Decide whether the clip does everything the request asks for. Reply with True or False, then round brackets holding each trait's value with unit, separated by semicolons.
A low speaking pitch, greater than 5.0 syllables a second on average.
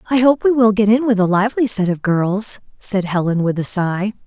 False (210 Hz; 5.3 syllables/s)